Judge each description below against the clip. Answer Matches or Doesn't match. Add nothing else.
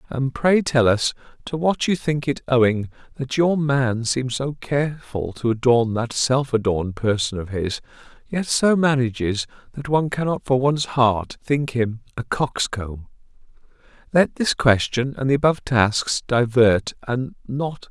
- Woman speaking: Doesn't match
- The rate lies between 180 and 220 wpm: Doesn't match